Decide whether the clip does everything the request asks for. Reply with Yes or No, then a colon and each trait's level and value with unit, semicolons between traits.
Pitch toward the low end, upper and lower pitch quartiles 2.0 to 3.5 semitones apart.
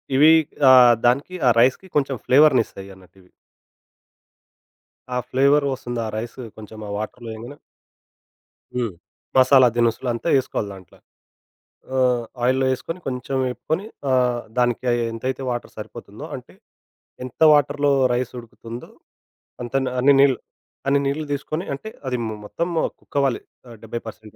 Yes: low, 125 Hz; average, 2.9 semitones